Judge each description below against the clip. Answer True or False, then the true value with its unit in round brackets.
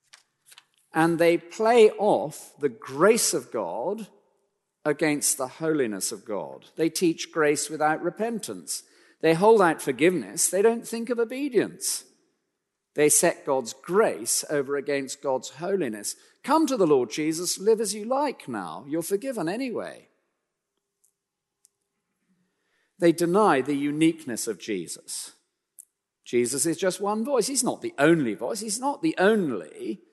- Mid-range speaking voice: False (195 Hz)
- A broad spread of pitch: True (6.6 semitones)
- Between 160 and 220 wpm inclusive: False (135 wpm)